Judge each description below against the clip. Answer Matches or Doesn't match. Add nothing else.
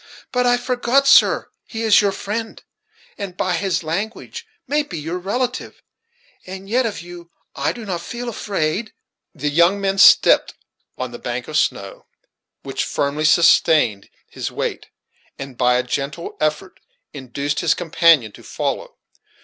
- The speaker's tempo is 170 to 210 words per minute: Doesn't match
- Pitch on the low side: Doesn't match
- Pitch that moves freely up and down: Matches